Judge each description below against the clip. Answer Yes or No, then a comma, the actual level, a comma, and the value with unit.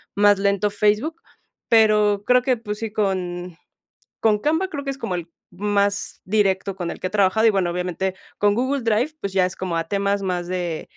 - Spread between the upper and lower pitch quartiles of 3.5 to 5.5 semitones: No, average, 3.0 semitones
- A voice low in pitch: No, high, 200 Hz